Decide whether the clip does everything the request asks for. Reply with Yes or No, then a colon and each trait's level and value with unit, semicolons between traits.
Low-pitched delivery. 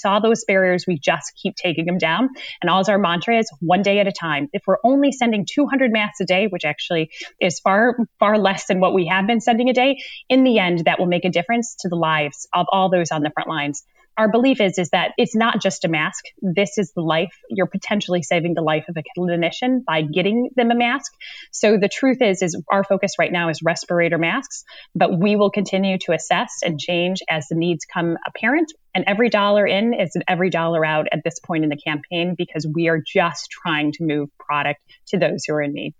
No: medium, 185 Hz